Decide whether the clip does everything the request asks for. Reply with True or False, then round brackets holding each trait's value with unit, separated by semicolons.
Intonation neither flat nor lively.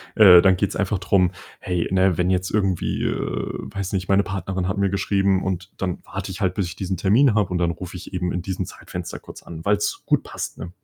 False (1.6 semitones)